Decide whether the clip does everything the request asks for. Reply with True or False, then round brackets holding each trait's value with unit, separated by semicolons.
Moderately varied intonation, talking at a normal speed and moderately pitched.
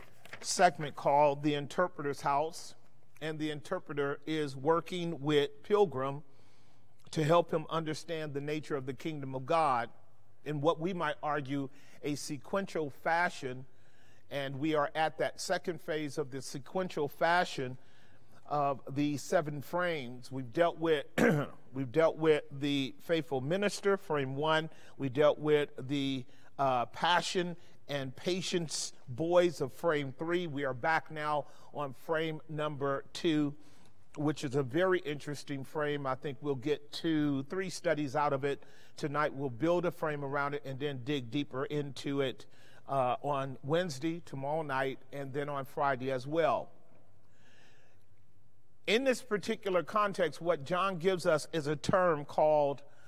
True (3.2 semitones; 145 wpm; 145 Hz)